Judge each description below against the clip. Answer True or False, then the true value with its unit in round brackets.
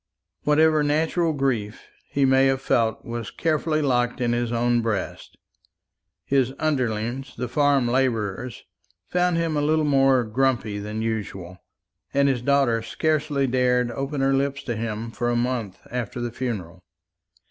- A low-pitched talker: True (125 Hz)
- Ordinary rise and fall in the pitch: True (3.3 semitones)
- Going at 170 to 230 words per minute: False (145 wpm)